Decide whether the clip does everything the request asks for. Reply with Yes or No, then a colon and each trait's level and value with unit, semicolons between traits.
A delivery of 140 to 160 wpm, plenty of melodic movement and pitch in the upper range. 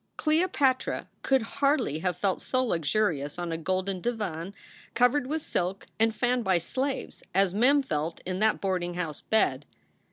Yes: average, 155 wpm; wide, 6.5 semitones; high, 195 Hz